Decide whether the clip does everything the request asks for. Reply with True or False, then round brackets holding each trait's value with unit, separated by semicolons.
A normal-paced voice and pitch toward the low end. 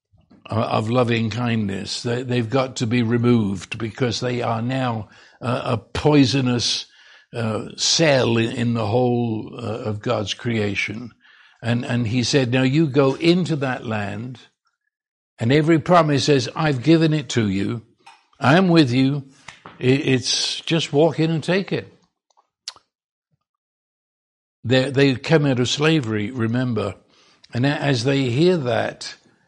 False (125 wpm; 125 Hz)